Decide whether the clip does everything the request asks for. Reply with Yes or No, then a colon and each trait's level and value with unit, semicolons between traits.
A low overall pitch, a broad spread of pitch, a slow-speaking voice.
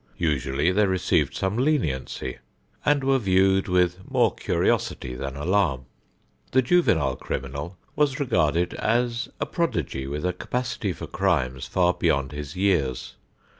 Yes: very low, 90 Hz; wide, 7.6 semitones; slow, 130 wpm